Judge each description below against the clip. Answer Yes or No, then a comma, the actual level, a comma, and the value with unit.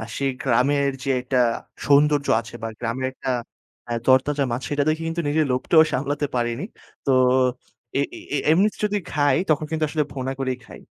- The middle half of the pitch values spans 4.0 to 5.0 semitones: No, narrow, 2.5 semitones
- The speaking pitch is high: No, medium, 140 Hz